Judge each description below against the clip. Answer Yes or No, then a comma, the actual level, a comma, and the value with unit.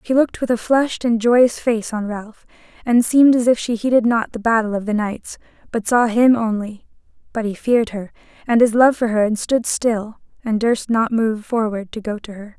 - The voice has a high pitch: Yes, high, 225 Hz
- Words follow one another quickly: Yes, fast, 225 wpm